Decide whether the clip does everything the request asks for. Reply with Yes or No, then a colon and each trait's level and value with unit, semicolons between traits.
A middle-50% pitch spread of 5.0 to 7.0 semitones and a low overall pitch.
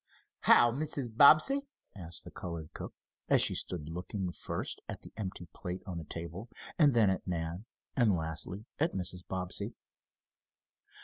Yes: wide, 5.4 semitones; very low, 95 Hz